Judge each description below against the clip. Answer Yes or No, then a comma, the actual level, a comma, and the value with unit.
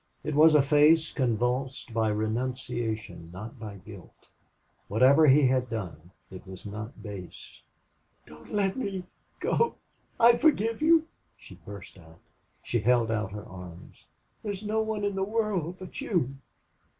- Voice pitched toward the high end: No, low, 125 Hz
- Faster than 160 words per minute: No, average, 145 wpm